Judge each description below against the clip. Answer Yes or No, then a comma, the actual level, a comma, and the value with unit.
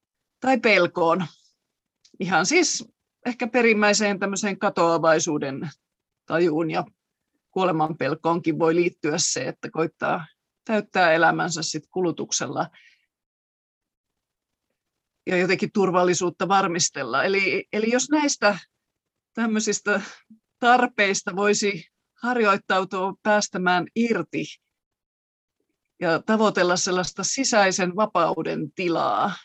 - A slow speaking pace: Yes, slow, 80 wpm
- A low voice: No, high, 190 Hz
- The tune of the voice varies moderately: Yes, average, 3.9 semitones